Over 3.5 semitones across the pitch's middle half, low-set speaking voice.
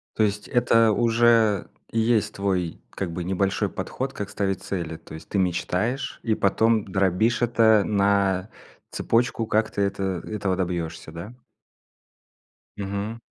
No: average, 3.0 semitones; low, 100 Hz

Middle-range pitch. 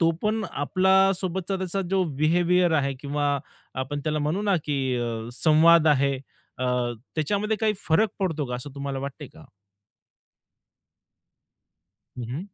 Yes: medium, 160 Hz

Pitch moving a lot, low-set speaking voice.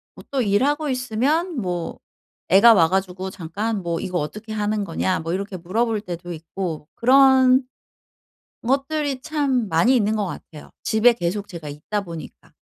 No: wide, 6.2 semitones; high, 210 Hz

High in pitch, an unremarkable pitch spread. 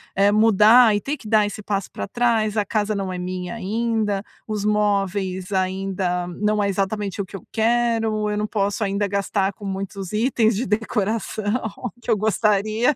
No: high, 210 Hz; narrow, 1.9 semitones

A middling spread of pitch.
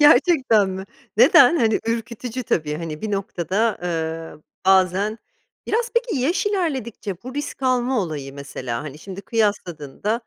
No: wide, 7.3 semitones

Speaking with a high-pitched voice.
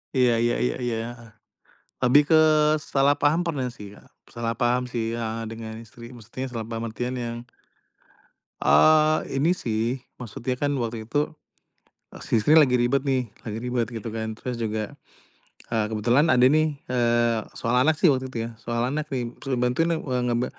No: low, 125 Hz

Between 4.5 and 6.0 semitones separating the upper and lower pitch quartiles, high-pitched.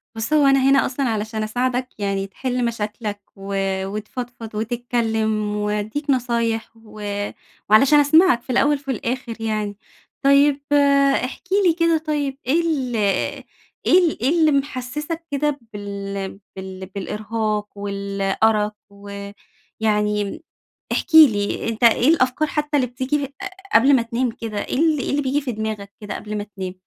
Yes: average, 4.8 semitones; high, 230 Hz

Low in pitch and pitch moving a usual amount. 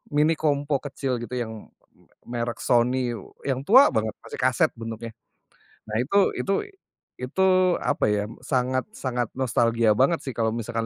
Yes: low, 125 Hz; average, 3.3 semitones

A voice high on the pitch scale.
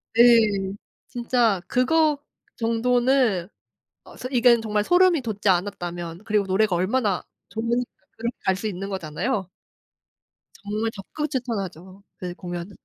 Yes: high, 215 Hz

